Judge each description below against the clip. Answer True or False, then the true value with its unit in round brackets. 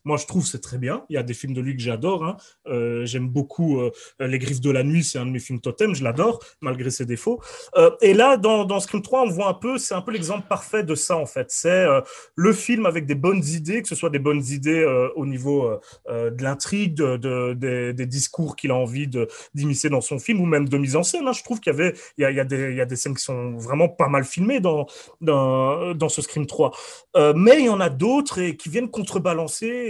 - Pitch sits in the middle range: True (150 Hz)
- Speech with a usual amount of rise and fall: False (7.1 semitones)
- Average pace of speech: False (255 wpm)